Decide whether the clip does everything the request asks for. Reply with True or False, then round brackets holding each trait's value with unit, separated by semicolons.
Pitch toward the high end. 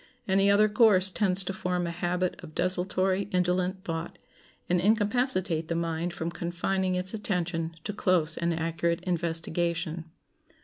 False (180 Hz)